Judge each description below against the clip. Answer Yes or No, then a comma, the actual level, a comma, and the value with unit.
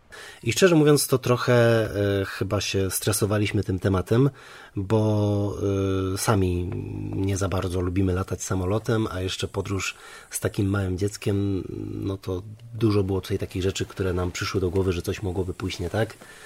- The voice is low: Yes, low, 100 Hz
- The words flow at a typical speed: No, fast, 165 wpm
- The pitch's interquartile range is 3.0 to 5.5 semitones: No, narrow, 2.4 semitones